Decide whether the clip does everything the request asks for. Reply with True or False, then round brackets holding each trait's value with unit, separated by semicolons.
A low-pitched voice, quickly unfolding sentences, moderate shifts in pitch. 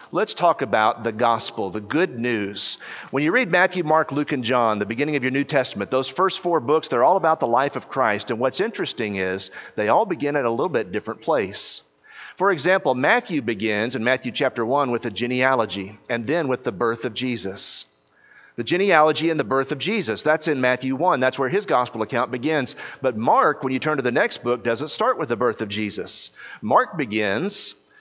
True (130 Hz; 210 wpm; 4.7 semitones)